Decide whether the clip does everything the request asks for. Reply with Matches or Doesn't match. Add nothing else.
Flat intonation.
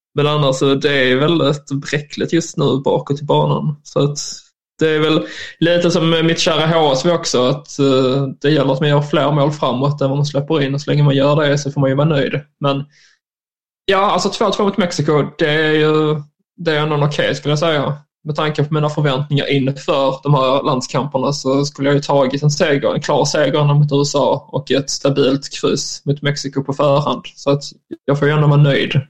Matches